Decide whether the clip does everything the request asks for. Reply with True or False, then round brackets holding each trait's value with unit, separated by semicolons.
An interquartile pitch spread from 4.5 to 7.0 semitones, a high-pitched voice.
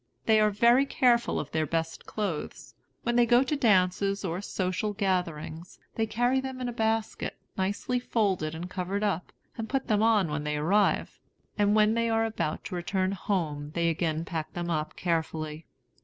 True (5.1 semitones; 195 Hz)